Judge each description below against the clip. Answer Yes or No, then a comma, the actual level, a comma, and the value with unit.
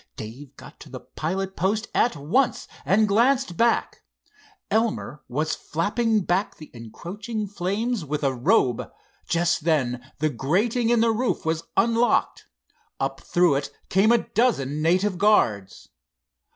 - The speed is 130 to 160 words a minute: Yes, average, 140 wpm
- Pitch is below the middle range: No, medium, 185 Hz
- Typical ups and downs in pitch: No, wide, 7.2 semitones